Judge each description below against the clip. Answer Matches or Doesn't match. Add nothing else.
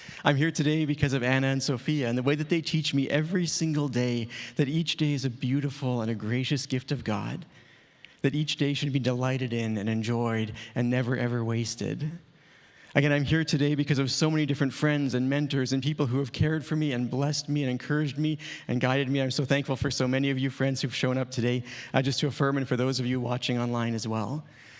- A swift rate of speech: Matches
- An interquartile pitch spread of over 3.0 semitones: Doesn't match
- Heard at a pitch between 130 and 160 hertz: Matches